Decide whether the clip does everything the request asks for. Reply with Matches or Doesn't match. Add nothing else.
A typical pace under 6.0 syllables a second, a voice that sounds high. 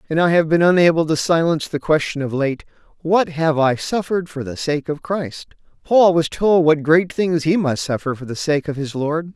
Doesn't match